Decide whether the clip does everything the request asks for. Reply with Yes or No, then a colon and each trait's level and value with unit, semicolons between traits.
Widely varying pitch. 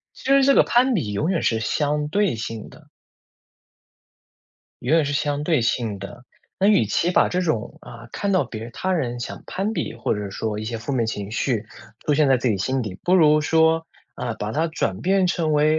Yes: wide, 6.6 semitones